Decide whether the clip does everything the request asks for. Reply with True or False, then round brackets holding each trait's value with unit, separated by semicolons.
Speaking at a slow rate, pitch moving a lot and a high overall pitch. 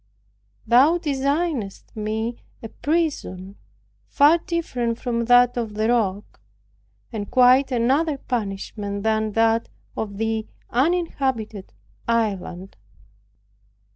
False (95 wpm; 4.1 semitones; 235 Hz)